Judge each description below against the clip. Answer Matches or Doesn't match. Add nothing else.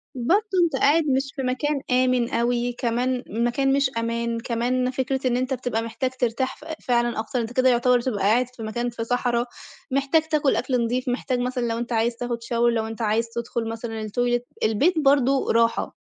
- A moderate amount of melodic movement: Doesn't match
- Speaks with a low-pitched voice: Doesn't match